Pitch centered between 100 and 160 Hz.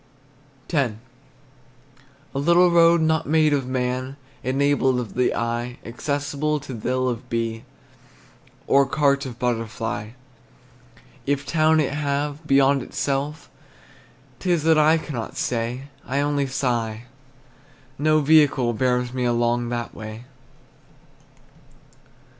Yes: low, 135 Hz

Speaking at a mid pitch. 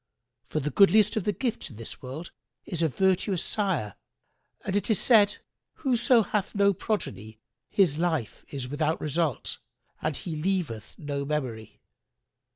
Yes: medium, 170 Hz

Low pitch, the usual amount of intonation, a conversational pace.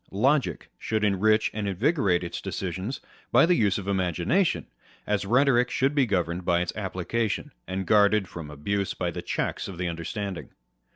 Yes: low, 100 Hz; average, 3.8 semitones; average, 165 wpm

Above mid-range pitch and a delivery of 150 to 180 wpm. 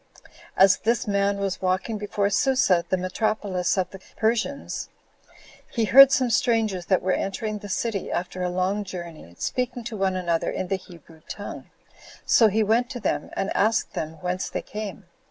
Yes: high, 200 Hz; average, 175 wpm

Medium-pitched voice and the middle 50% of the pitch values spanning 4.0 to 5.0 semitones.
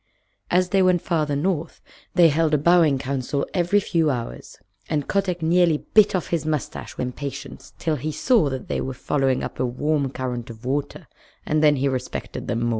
Yes: medium, 150 Hz; average, 4.4 semitones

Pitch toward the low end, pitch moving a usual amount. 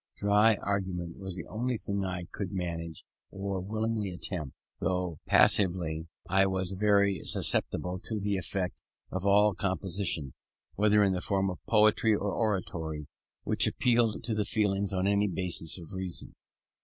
No: very low, 95 Hz; narrow, 2.3 semitones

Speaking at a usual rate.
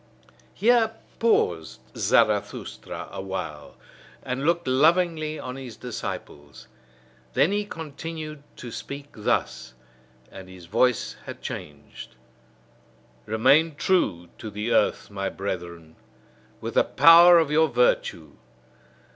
No: slow, 105 wpm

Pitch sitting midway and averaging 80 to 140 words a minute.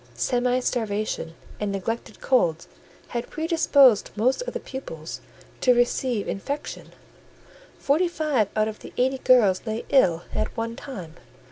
No: high, 240 Hz; slow, 135 wpm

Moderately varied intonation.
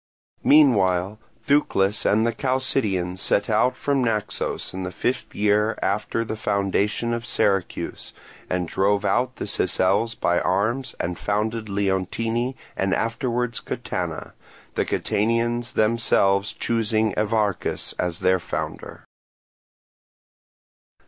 Yes: average, 3.2 semitones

